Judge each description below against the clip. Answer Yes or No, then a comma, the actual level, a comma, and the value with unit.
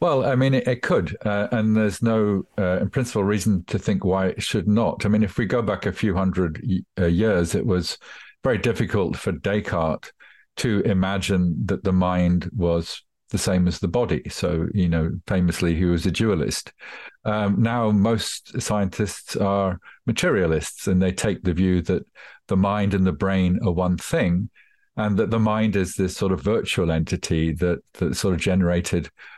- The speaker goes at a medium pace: Yes, average, 190 wpm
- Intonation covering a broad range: No, average, 2.9 semitones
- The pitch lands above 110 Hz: No, very low, 95 Hz